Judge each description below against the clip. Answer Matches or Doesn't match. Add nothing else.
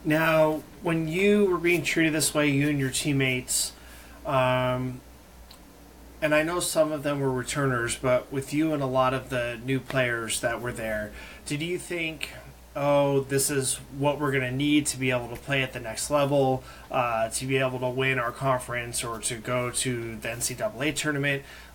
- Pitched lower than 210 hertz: Matches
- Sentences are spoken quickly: Doesn't match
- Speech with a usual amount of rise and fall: Matches